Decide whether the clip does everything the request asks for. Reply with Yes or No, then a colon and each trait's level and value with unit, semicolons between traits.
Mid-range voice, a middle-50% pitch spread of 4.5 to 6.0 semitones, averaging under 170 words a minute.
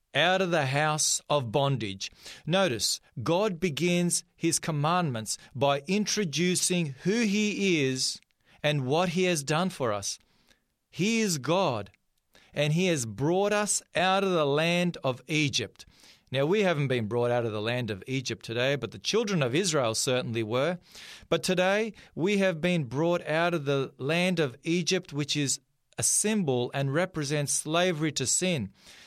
Yes: medium, 155 Hz; wide, 5.5 semitones; average, 160 wpm